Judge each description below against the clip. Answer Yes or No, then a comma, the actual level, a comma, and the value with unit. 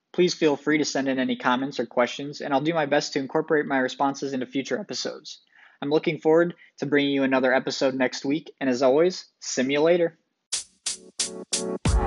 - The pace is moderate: Yes, average, 180 wpm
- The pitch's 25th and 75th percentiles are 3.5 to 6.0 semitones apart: No, average, 2.9 semitones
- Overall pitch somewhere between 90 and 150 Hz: Yes, medium, 140 Hz